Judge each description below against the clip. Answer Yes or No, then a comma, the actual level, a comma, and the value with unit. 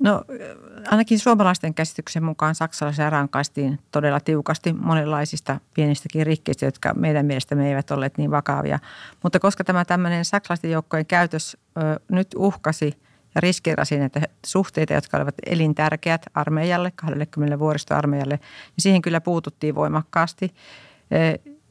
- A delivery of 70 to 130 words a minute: Yes, average, 125 wpm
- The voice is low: No, medium, 155 Hz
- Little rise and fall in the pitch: No, average, 3.1 semitones